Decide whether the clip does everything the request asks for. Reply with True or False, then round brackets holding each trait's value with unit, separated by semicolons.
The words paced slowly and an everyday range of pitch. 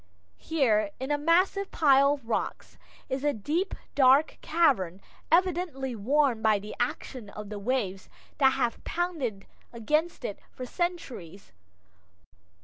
False (130 wpm; 6.5 semitones)